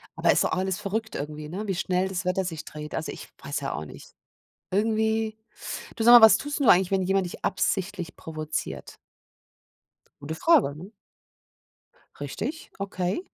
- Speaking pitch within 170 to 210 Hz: Yes, high, 190 Hz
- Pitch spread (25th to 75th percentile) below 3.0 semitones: No, average, 5.3 semitones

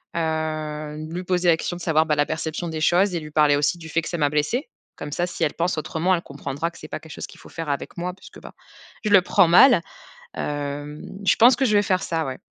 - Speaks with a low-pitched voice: No, medium, 160 Hz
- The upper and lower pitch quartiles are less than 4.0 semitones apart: Yes, average, 2.9 semitones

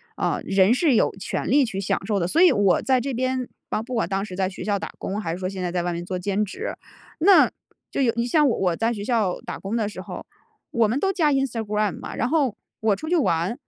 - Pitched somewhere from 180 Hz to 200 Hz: No, high, 215 Hz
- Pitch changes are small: No, average, 5.2 semitones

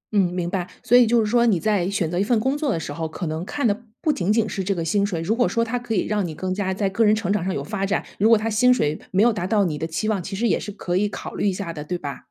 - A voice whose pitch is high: Yes, high, 200 Hz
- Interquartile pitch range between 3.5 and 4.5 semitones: Yes, average, 3.8 semitones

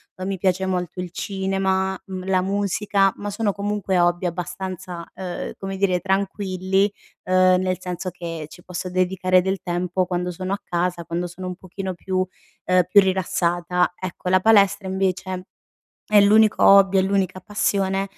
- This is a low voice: No, medium, 185 Hz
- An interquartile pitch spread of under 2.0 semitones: Yes, narrow, 1.3 semitones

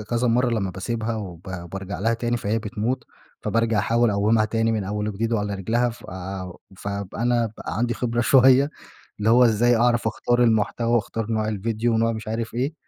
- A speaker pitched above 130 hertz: No, low, 115 Hz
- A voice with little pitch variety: Yes, narrow, 2.3 semitones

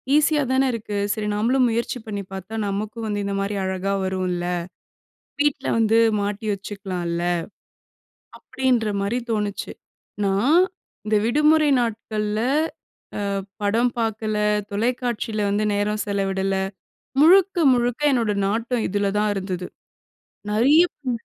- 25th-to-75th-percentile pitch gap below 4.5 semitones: Yes, average, 3.2 semitones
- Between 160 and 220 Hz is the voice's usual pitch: Yes, high, 215 Hz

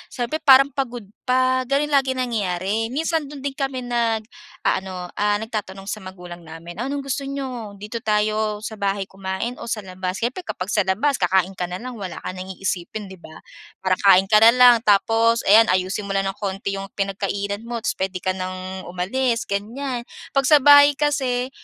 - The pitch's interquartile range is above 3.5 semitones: Yes, average, 5.1 semitones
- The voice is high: Yes, high, 215 Hz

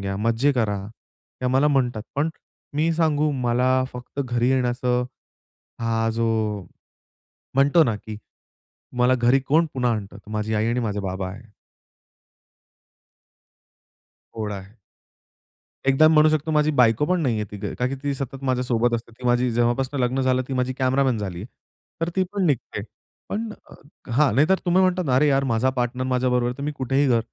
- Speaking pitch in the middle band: No, low, 125 Hz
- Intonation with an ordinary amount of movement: Yes, average, 3.5 semitones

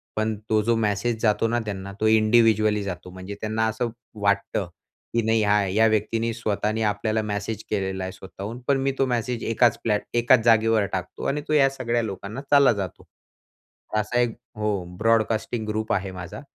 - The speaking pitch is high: No, low, 110 Hz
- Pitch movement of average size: No, narrow, 2.2 semitones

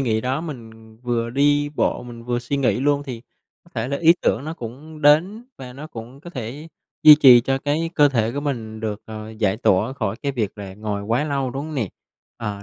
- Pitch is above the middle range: No, low, 125 Hz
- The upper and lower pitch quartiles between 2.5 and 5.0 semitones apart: Yes, average, 4.5 semitones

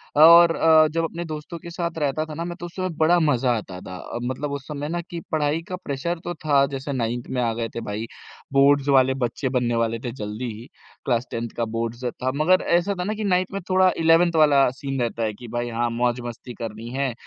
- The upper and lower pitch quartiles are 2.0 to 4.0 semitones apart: No, wide, 5.6 semitones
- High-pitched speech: No, medium, 140 Hz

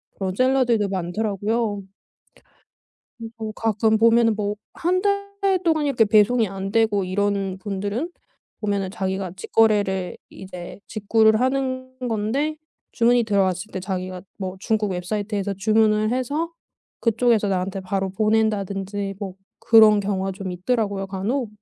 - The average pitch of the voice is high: Yes, high, 210 Hz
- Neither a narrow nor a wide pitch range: Yes, average, 3.0 semitones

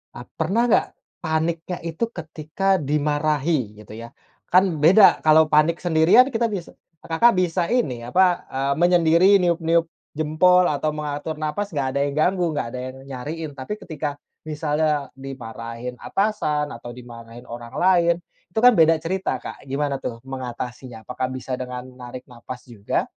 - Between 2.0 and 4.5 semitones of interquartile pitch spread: No, average, 5.0 semitones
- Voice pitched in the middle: Yes, medium, 155 Hz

